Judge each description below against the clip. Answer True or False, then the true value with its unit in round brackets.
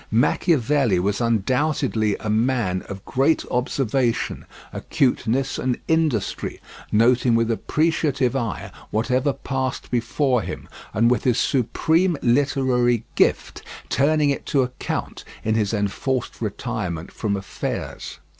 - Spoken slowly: True (115 wpm)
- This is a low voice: True (125 Hz)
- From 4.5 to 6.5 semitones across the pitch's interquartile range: False (3.6 semitones)